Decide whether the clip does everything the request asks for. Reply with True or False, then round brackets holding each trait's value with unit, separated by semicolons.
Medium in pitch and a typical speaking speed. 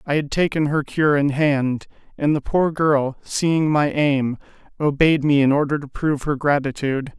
True (145 Hz; 185 wpm)